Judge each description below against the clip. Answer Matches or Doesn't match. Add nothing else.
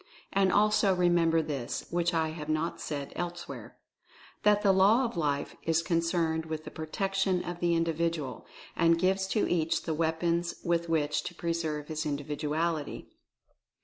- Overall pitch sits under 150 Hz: Doesn't match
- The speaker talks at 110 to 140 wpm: Doesn't match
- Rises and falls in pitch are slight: Matches